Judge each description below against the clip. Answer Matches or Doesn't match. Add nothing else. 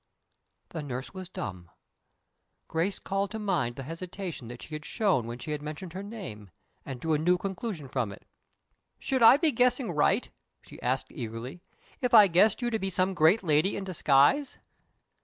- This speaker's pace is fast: Doesn't match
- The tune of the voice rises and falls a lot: Matches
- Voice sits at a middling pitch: Matches